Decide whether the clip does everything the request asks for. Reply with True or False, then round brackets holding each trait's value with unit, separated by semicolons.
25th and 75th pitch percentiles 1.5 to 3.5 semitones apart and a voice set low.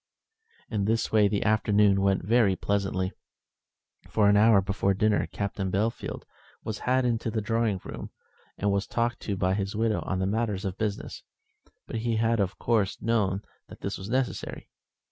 True (2.5 semitones; 105 Hz)